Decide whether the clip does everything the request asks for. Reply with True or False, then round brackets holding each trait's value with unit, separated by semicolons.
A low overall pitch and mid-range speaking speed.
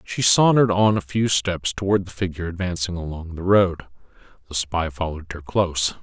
True (90 Hz; 180 wpm)